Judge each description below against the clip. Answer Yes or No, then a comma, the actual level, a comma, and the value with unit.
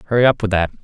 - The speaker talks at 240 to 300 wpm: Yes, fast, 285 wpm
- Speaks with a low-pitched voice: Yes, low, 105 Hz